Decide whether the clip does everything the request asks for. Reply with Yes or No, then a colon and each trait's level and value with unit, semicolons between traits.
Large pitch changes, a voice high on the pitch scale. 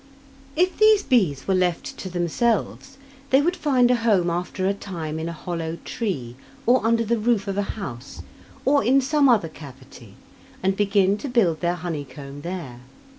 Yes: wide, 6.6 semitones; high, 195 Hz